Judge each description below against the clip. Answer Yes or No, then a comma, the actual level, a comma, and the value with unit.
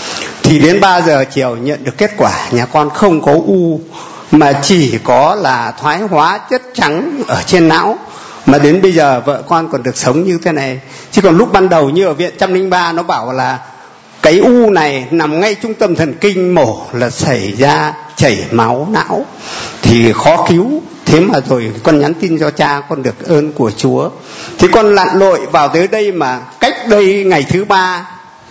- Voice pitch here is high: No, medium, 160 Hz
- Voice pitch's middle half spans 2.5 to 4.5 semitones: No, average, 5.1 semitones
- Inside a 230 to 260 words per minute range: No, average, 200 wpm